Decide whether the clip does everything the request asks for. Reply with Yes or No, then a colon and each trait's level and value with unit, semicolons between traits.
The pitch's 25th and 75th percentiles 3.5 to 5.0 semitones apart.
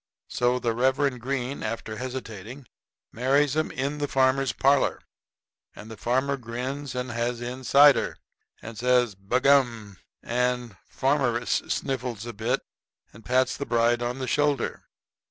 No: narrow, 2.4 semitones